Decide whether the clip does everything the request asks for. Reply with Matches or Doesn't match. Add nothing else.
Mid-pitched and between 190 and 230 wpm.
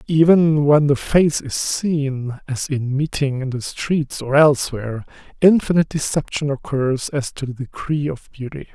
Doesn't match